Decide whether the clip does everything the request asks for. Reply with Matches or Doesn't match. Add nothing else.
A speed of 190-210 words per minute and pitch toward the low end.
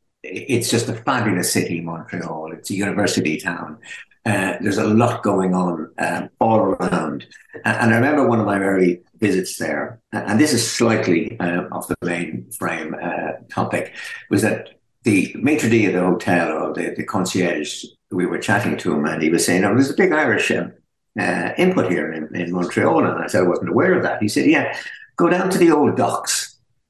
Matches